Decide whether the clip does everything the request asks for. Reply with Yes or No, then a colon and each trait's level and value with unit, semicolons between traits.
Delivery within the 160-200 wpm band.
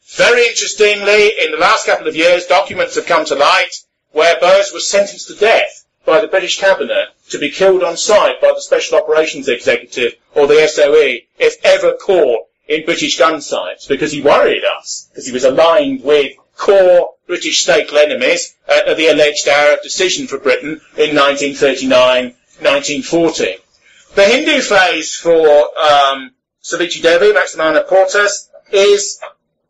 No: average, 150 wpm